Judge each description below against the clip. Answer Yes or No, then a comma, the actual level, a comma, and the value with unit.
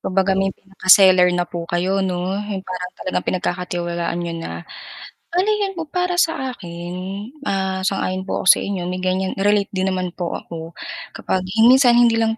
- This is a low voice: No, high, 190 Hz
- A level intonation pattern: Yes, narrow, 2.3 semitones